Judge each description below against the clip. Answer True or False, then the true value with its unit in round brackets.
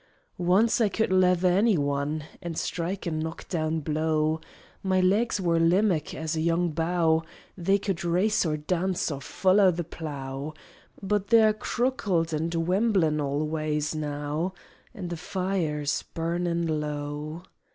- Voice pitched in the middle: True (170 Hz)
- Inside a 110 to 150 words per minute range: True (140 wpm)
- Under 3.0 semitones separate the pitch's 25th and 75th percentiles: False (3.3 semitones)